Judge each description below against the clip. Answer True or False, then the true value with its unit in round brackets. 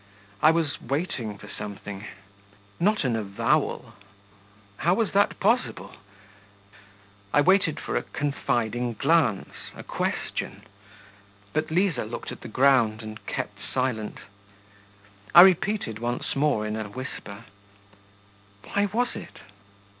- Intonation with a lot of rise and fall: True (7.6 semitones)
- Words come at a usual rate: False (115 wpm)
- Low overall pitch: True (130 Hz)